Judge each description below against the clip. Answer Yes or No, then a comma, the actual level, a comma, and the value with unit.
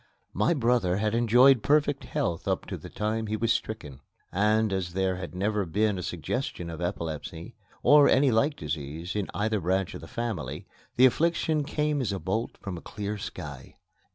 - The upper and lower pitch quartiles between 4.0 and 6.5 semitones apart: Yes, average, 5.2 semitones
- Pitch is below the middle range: Yes, low, 105 Hz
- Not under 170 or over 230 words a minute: Yes, average, 180 wpm